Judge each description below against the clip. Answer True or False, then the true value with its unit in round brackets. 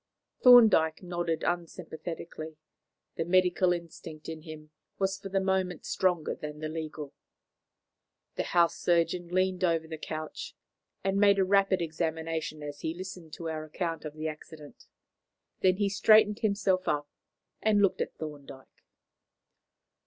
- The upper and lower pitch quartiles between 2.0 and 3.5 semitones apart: True (3.1 semitones)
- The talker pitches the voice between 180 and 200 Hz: False (170 Hz)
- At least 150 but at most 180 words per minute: False (140 wpm)